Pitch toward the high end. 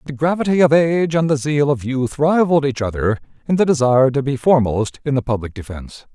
No: medium, 140 Hz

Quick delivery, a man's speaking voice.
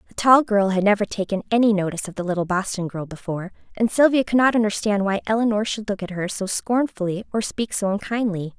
No: fast, 215 wpm; female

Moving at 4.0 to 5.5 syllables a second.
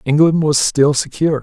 Yes: 5.3 syllables/s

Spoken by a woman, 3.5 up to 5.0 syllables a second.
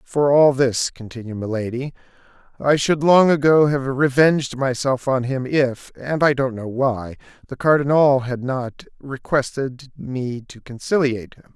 No: male; 4.3 syllables/s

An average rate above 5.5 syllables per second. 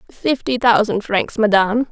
No: 4.8 syllables/s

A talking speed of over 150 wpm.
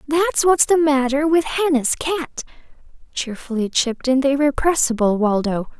No: slow, 135 wpm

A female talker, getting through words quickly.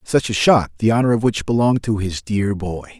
No: male; fast, 240 wpm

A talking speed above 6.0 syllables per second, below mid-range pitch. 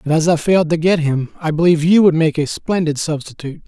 No: 6.4 syllables/s; medium, 160 Hz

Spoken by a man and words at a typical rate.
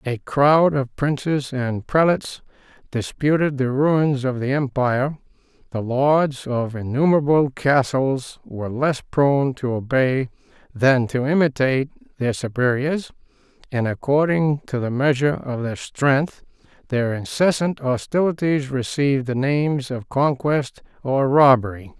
No: male; slow, 125 wpm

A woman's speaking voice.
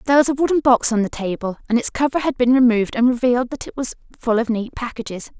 Yes: female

